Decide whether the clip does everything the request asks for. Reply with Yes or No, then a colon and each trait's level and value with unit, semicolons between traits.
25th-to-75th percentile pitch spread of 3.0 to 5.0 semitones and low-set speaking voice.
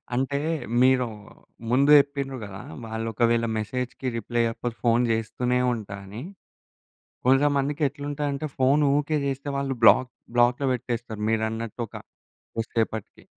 Yes: average, 3.4 semitones; low, 125 Hz